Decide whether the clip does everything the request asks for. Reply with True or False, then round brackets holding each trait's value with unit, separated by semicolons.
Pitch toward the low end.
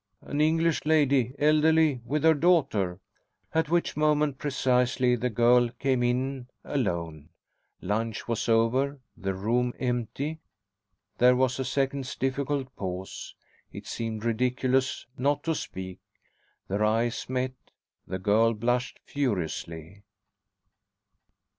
True (125 Hz)